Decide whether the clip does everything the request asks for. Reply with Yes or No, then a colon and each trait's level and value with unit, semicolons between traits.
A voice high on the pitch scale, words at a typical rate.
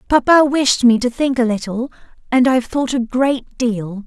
Yes: very high, 250 Hz; average, 175 wpm